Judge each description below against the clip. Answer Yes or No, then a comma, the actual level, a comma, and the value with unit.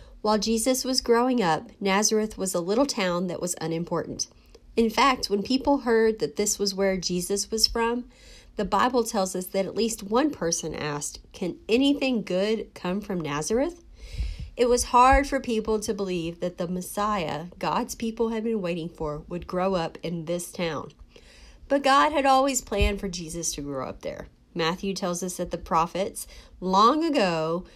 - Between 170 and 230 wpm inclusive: Yes, average, 175 wpm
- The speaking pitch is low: No, high, 200 Hz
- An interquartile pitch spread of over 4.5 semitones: Yes, average, 5.0 semitones